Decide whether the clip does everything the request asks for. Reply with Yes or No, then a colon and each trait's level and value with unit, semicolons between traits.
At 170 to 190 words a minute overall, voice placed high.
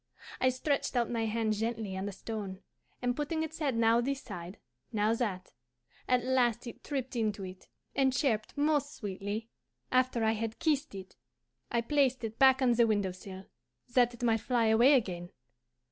Yes: average, 175 wpm; high, 230 Hz